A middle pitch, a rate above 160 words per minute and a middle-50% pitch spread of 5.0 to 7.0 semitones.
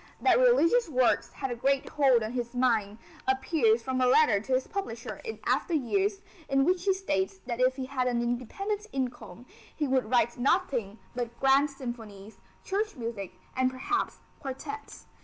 No: very high, 260 Hz; average, 170 wpm; average, 5.3 semitones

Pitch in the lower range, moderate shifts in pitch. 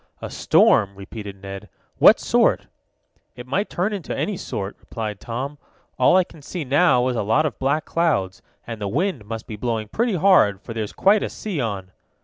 No: low, 125 Hz; wide, 8.4 semitones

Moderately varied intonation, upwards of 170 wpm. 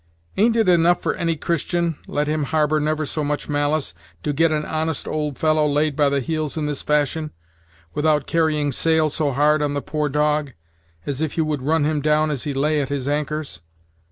No: narrow, 1.3 semitones; fast, 205 wpm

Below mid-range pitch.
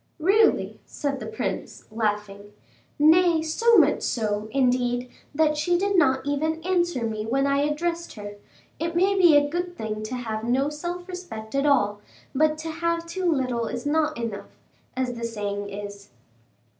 No: very high, 285 Hz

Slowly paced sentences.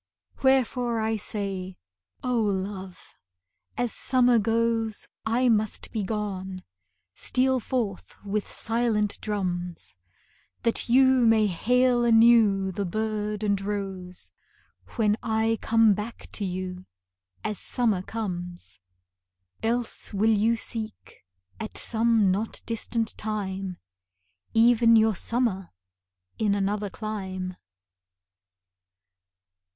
Yes: slow, 100 wpm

